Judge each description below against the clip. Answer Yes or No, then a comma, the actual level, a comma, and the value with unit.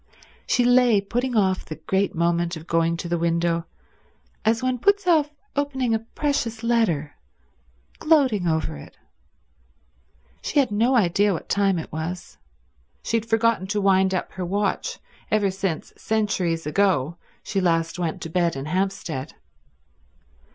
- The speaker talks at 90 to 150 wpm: Yes, average, 145 wpm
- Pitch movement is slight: No, average, 5.3 semitones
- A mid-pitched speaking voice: No, high, 195 Hz